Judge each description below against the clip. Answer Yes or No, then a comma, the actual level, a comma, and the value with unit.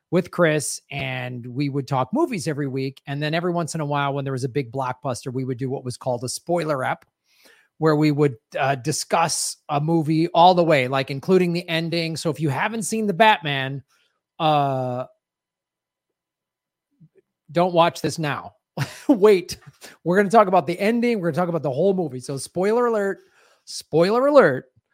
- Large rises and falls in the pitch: No, average, 4.6 semitones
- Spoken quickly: No, average, 190 wpm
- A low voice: No, medium, 160 Hz